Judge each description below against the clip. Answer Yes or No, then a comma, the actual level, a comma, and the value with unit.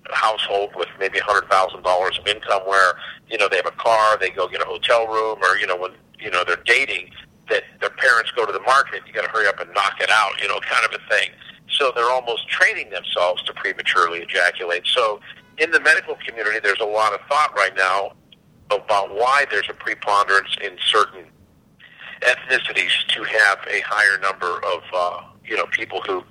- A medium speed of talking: No, fast, 210 wpm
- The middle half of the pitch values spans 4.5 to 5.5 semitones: No, average, 3.2 semitones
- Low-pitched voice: Yes, low, 105 Hz